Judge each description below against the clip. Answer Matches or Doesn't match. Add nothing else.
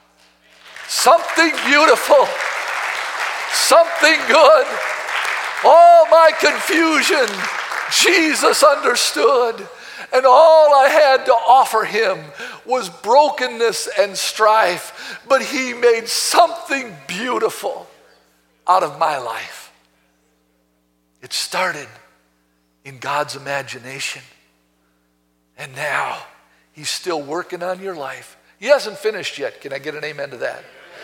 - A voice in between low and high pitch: Doesn't match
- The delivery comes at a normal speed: Doesn't match